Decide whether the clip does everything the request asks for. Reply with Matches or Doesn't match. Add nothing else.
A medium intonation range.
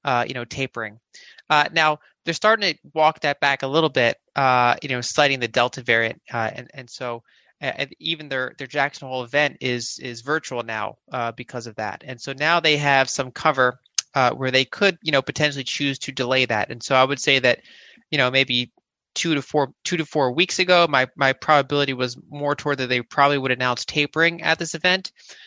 Matches